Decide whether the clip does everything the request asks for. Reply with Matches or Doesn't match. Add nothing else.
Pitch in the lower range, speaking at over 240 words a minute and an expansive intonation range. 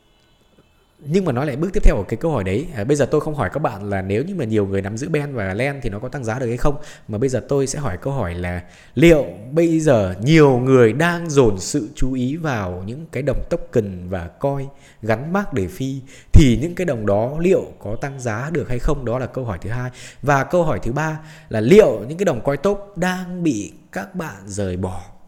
Matches